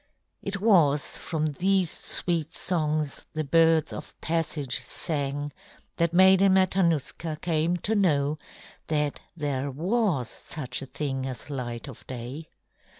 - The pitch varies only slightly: No, average, 3.6 semitones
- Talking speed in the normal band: No, slow, 125 wpm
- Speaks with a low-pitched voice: No, medium, 155 Hz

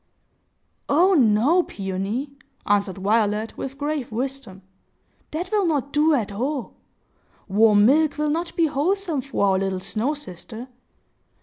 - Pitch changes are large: Yes, wide, 6.5 semitones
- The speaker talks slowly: Yes, slow, 130 wpm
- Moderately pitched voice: No, very high, 265 Hz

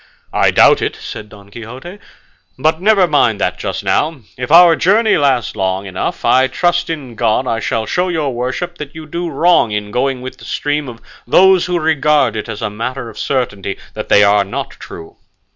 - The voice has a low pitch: Yes, low, 130 Hz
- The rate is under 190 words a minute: No, average, 195 wpm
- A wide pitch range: Yes, wide, 6.8 semitones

